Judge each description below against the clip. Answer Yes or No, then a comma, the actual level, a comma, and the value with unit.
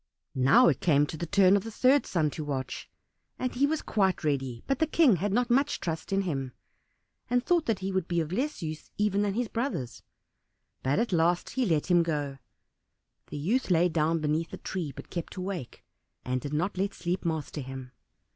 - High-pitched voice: No, medium, 175 Hz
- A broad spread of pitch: Yes, wide, 5.9 semitones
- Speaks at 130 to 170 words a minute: No, fast, 205 wpm